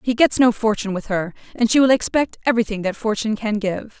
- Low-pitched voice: No, high, 220 Hz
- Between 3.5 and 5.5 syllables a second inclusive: No, 6.3 syllables/s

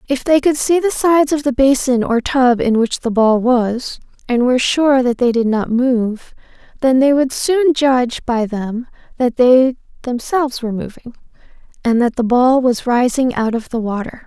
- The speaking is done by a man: No, female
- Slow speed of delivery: No, average, 195 wpm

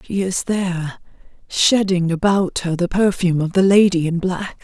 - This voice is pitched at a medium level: Yes, medium, 180 Hz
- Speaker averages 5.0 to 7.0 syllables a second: No, 4.8 syllables/s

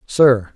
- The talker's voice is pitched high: No, low, 120 Hz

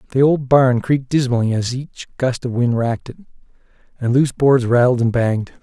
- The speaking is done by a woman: No, male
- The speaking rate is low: No, average, 190 wpm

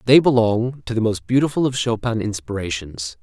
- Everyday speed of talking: Yes, average, 170 wpm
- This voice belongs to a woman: No, male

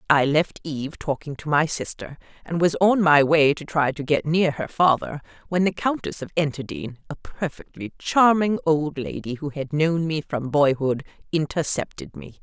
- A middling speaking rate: Yes, average, 180 wpm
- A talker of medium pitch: Yes, medium, 155 Hz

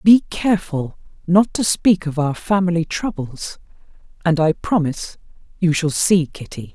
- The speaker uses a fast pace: No, slow, 135 wpm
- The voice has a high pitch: No, medium, 170 Hz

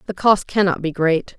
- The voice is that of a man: No, female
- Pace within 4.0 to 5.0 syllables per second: Yes, 4.9 syllables/s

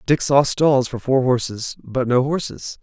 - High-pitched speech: No, low, 130 Hz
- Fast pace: No, average, 190 wpm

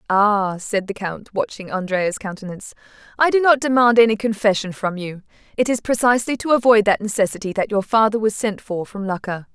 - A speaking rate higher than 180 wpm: Yes, average, 190 wpm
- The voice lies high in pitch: Yes, high, 210 Hz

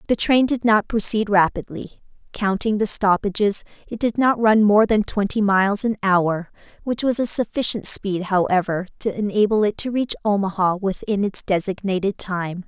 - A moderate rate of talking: Yes, average, 165 wpm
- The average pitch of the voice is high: Yes, high, 205 Hz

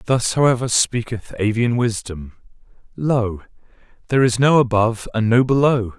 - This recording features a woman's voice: No, male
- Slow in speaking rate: Yes, slow, 120 wpm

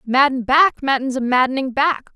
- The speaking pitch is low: No, very high, 265 Hz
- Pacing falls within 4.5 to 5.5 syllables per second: Yes, 5.0 syllables/s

